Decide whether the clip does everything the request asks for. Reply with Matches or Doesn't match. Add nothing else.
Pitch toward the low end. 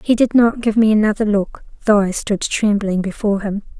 Doesn't match